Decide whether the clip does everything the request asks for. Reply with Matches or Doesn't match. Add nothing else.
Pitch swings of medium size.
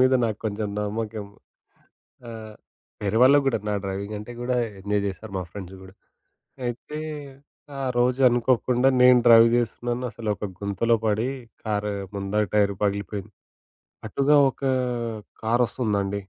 Matches